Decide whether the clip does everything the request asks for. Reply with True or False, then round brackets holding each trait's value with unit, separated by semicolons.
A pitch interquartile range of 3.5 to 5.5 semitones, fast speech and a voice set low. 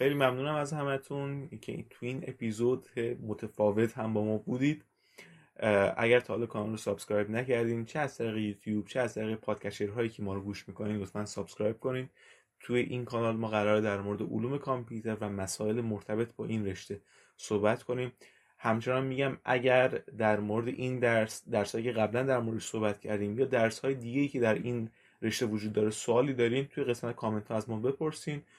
False (3.1 semitones; 185 wpm; 115 Hz)